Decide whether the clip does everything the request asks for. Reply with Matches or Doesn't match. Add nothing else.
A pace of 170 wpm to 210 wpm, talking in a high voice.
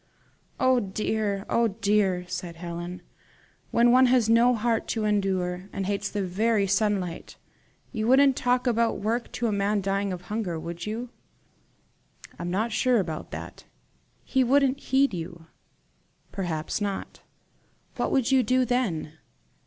Doesn't match